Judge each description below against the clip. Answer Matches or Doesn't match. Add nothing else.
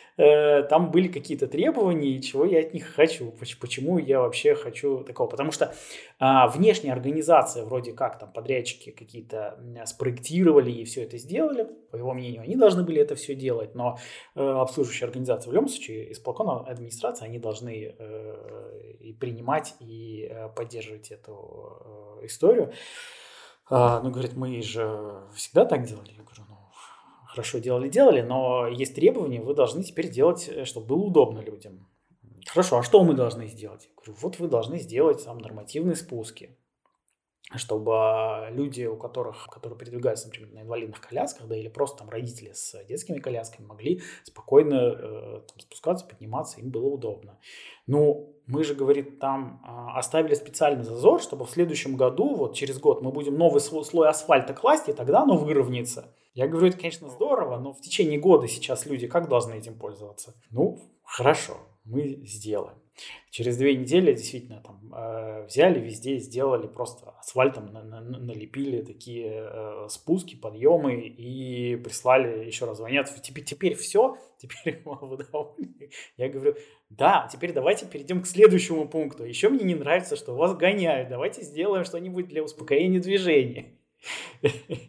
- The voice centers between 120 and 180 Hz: Matches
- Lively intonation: Matches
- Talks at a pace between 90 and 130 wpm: Doesn't match